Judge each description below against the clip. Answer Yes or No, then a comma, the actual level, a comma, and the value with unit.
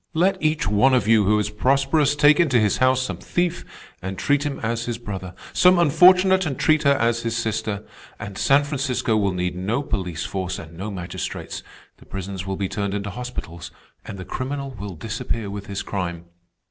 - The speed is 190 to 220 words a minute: Yes, average, 195 wpm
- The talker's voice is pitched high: No, low, 115 Hz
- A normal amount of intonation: No, wide, 6.2 semitones